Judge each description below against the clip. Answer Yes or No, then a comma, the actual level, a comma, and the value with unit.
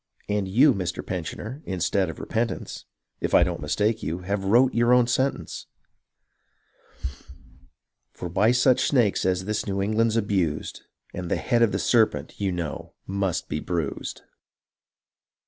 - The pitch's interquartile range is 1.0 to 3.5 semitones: No, average, 4.2 semitones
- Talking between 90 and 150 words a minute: Yes, average, 145 wpm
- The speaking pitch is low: Yes, low, 100 Hz